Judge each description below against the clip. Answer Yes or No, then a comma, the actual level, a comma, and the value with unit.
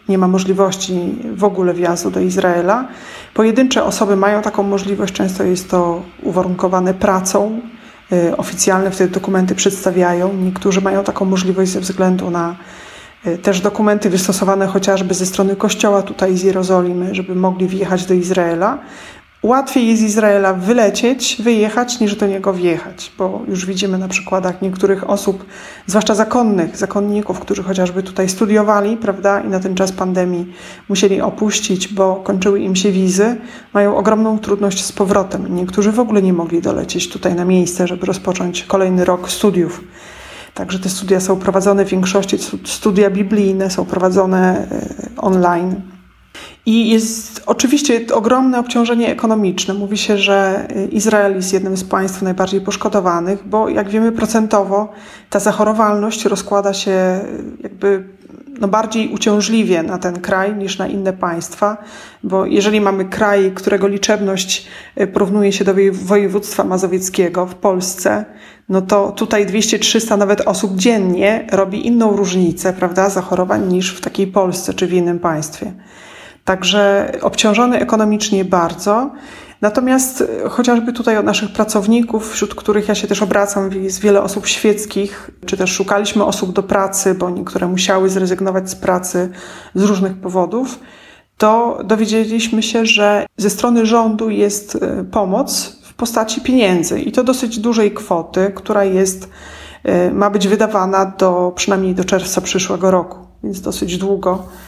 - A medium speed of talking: Yes, average, 140 wpm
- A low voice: No, high, 195 Hz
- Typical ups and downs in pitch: No, narrow, 2.1 semitones